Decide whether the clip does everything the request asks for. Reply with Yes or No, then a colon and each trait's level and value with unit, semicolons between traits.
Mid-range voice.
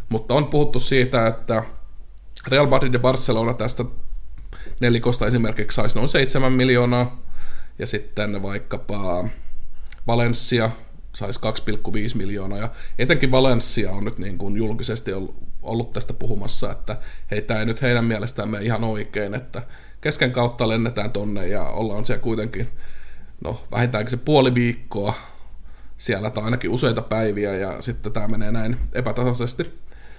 No: low, 115 Hz